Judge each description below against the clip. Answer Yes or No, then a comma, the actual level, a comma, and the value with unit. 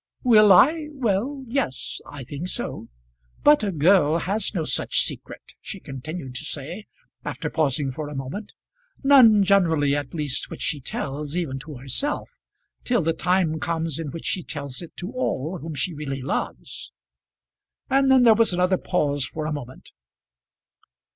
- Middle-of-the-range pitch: Yes, medium, 165 Hz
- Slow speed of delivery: No, average, 160 wpm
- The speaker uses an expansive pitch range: Yes, wide, 6.2 semitones